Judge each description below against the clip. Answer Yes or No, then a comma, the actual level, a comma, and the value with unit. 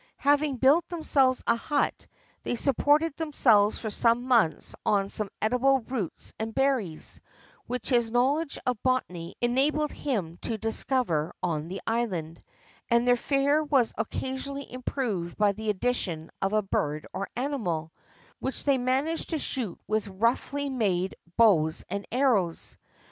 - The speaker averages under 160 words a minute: Yes, average, 140 wpm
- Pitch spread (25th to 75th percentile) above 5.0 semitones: Yes, wide, 5.4 semitones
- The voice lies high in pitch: Yes, high, 240 Hz